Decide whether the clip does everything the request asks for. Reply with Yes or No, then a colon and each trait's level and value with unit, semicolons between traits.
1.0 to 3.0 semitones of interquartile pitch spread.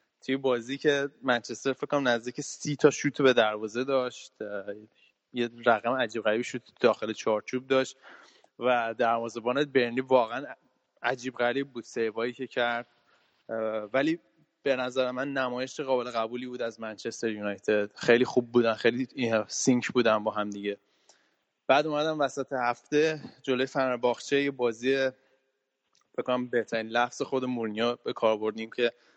Yes: narrow, 2.6 semitones